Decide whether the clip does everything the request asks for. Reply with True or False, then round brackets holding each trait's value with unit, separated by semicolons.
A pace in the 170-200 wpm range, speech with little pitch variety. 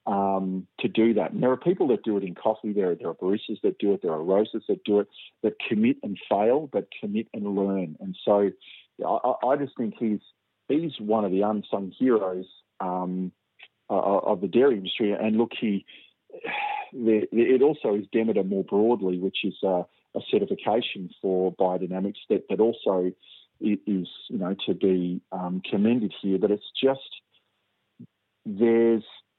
False (175 wpm; 3.1 semitones)